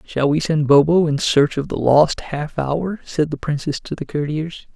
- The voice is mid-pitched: Yes, medium, 150 Hz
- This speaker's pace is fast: Yes, fast, 215 wpm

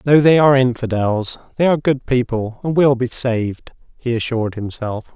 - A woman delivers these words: No, male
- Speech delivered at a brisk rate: No, average, 175 wpm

